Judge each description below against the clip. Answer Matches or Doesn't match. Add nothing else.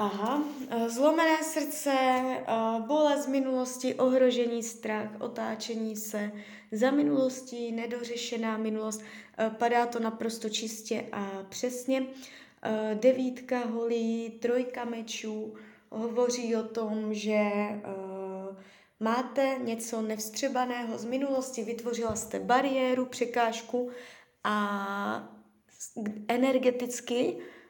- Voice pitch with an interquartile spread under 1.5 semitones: Doesn't match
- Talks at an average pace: Doesn't match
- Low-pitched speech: Doesn't match